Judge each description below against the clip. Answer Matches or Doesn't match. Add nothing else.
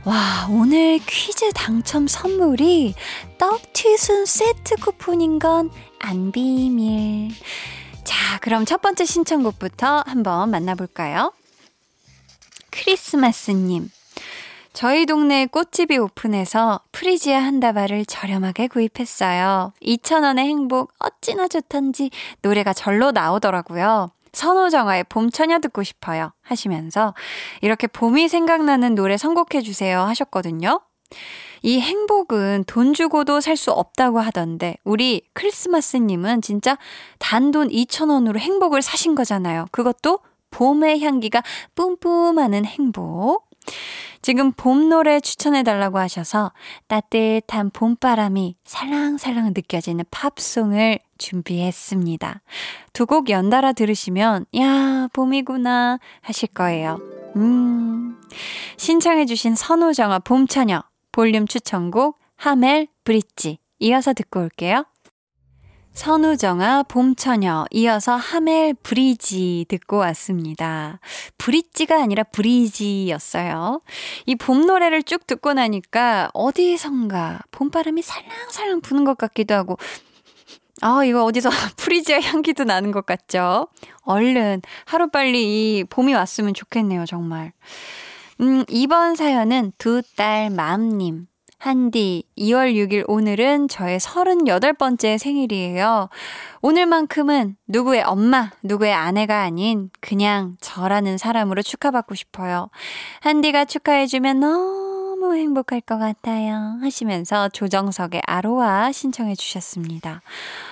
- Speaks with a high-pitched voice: Matches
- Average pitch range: Doesn't match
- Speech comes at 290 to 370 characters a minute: Doesn't match